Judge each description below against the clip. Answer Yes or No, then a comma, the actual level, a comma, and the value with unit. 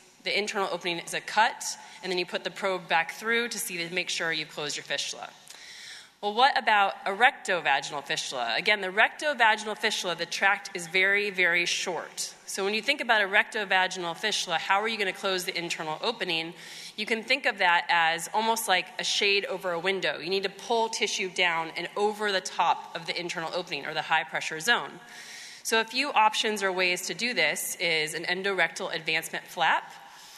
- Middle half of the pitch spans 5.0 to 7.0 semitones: No, average, 3.8 semitones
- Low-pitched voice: No, high, 190 Hz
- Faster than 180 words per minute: Yes, average, 200 wpm